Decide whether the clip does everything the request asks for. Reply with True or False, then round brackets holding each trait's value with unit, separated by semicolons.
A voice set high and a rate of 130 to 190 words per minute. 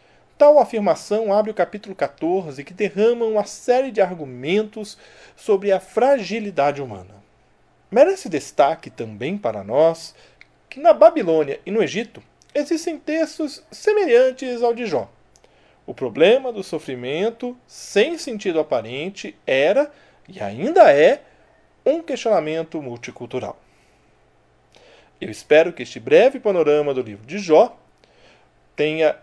False (205 Hz; 120 wpm)